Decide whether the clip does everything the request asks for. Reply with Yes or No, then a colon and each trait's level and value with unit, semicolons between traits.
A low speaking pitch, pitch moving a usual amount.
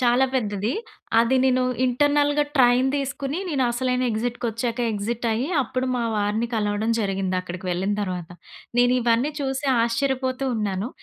No: high, 240 Hz; average, 3.7 semitones